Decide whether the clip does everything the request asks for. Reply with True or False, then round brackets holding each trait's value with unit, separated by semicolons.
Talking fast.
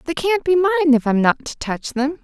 True (270 wpm)